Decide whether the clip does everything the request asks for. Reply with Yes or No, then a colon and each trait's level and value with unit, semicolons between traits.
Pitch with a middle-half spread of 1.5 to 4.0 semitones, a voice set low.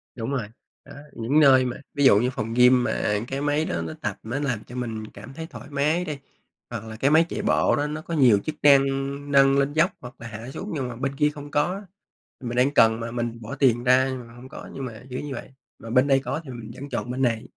Yes: average, 3.4 semitones; low, 130 Hz